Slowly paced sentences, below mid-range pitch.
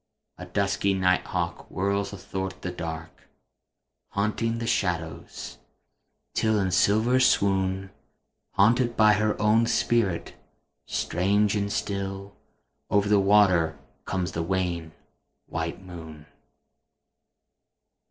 Yes: slow, 105 wpm; very low, 95 Hz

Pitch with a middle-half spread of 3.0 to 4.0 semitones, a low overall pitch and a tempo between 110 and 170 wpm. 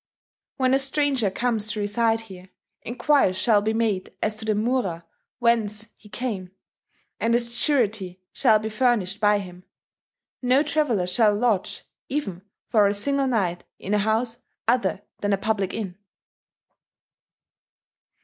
No: average, 3.4 semitones; high, 220 Hz; average, 140 wpm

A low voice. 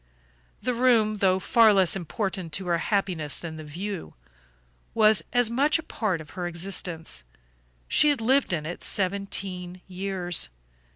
No: high, 190 Hz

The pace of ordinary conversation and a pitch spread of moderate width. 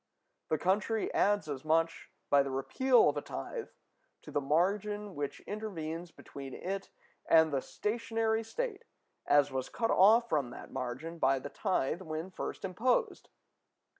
No: average, 150 wpm; wide, 6.8 semitones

